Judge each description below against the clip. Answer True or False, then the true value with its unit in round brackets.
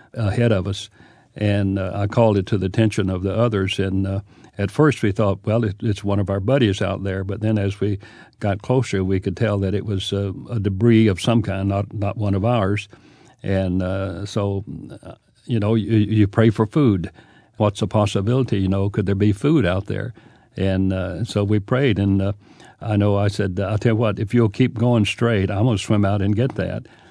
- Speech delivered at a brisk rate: True (220 wpm)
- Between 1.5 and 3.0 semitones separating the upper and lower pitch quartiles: True (2.4 semitones)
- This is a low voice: True (105 Hz)